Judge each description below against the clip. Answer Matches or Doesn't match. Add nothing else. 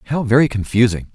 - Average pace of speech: Matches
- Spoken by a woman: Doesn't match